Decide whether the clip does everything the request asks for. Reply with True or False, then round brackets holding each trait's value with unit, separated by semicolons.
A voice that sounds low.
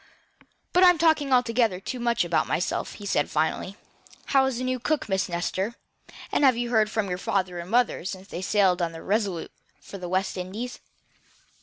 False (205 Hz)